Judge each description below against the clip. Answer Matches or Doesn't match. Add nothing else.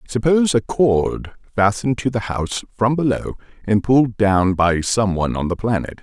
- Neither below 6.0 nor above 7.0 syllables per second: Doesn't match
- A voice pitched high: Doesn't match